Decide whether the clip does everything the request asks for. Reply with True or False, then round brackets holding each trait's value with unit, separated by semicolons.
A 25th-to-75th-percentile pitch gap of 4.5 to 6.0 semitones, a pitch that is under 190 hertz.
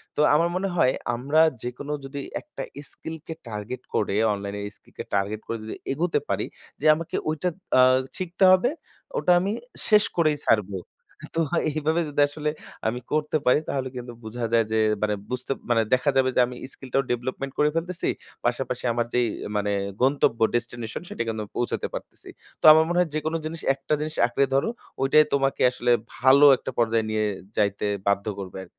True (5.1 semitones; 135 Hz)